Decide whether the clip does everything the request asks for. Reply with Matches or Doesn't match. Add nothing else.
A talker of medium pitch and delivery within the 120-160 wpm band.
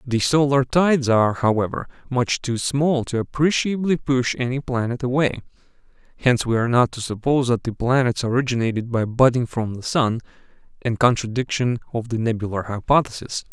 Doesn't match